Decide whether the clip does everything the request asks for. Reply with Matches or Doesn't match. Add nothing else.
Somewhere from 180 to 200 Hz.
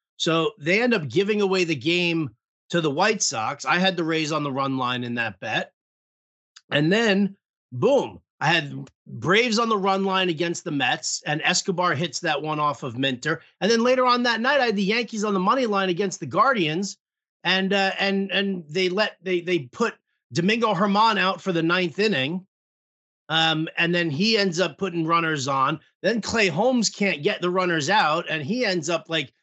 Matches